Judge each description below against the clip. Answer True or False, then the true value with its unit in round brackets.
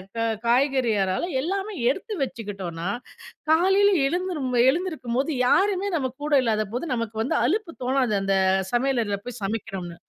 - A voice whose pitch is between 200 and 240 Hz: False (260 Hz)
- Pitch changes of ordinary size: False (8.1 semitones)